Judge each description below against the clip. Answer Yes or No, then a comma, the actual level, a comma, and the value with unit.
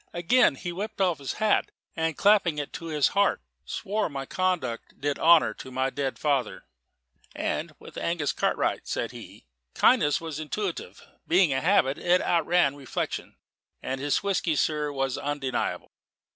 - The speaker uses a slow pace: No, average, 155 wpm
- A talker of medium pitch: Yes, medium, 155 Hz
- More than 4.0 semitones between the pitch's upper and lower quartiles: Yes, average, 4.5 semitones